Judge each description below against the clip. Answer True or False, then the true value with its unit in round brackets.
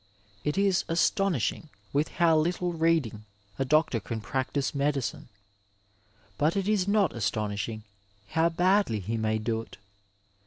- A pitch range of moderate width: False (7.5 semitones)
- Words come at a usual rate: False (130 wpm)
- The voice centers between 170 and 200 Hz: False (150 Hz)